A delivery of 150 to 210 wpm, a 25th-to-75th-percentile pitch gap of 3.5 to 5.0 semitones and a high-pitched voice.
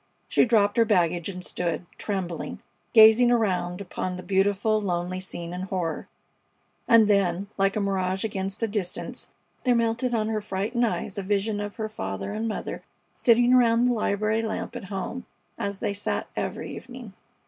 No: average, 170 wpm; average, 3.1 semitones; high, 205 Hz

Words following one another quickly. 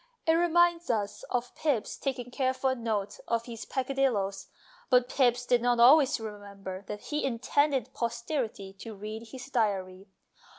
No: average, 140 wpm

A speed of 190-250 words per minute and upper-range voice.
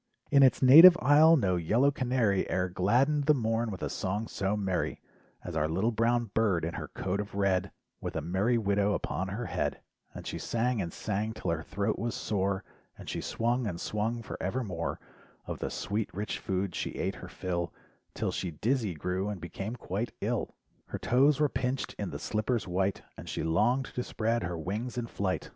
No: average, 195 wpm; low, 105 Hz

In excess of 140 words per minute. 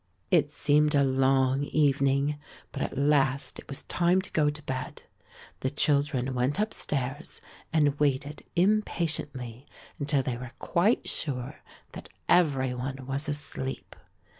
No: slow, 135 wpm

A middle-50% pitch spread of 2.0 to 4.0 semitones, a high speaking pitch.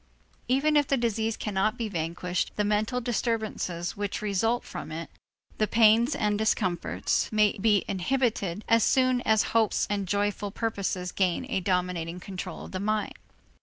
Yes: average, 3.4 semitones; high, 210 Hz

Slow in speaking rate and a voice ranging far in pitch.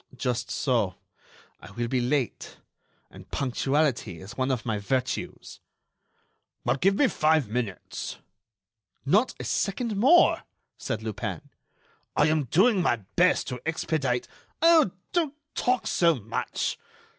Yes: slow, 125 wpm; wide, 7.7 semitones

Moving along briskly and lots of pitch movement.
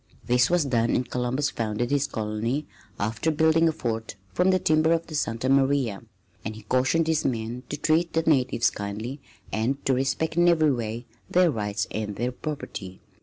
No: average, 180 wpm; wide, 5.7 semitones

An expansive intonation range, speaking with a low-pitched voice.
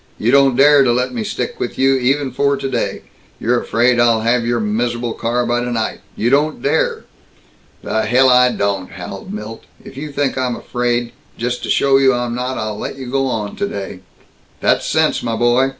No: narrow, 2.5 semitones; low, 120 Hz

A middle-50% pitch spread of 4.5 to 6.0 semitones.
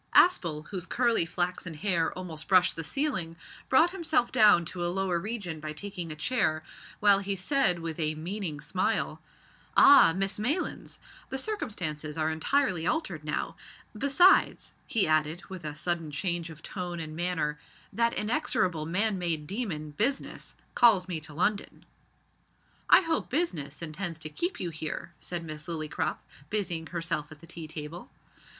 Yes: average, 5.1 semitones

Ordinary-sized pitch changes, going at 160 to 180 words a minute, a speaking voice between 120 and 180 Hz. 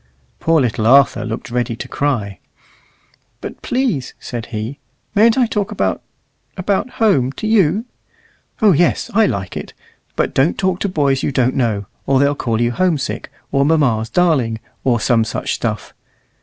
No: wide, 7.7 semitones; average, 165 wpm; medium, 140 Hz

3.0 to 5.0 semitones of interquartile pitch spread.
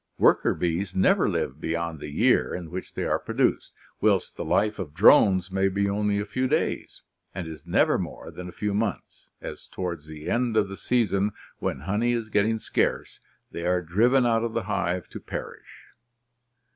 Yes: average, 3.8 semitones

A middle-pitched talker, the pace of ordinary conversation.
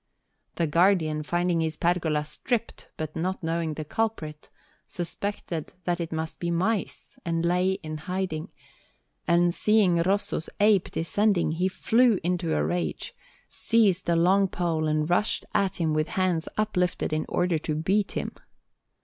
Yes: medium, 175 Hz; average, 150 wpm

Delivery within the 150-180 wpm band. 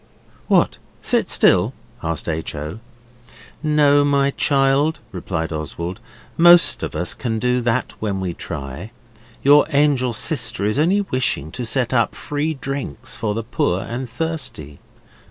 No: average, 140 wpm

